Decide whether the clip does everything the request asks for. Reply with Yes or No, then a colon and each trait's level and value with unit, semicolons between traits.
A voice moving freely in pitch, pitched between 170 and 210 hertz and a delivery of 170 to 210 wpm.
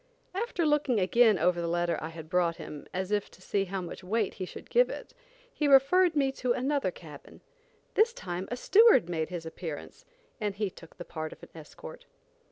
Yes: wide, 7.8 semitones; high, 190 Hz; average, 200 wpm